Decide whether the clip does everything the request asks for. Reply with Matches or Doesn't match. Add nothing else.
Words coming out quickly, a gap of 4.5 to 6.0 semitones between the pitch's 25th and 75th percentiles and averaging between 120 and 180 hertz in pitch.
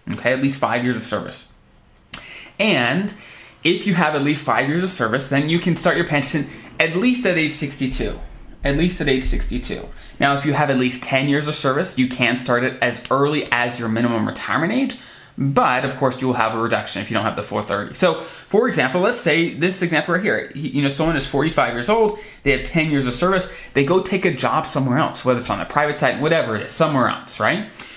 Matches